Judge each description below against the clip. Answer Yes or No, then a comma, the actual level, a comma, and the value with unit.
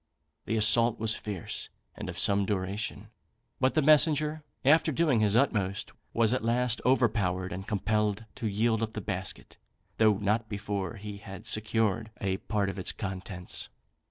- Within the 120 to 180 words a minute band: Yes, average, 155 wpm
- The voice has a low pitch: Yes, low, 110 Hz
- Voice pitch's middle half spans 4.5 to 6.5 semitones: No, average, 2.9 semitones